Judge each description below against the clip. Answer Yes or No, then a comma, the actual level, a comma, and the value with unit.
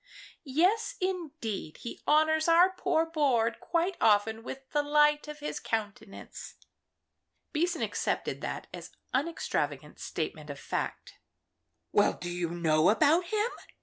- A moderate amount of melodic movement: No, wide, 8.3 semitones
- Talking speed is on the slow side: Yes, slow, 125 wpm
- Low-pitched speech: No, very high, 295 Hz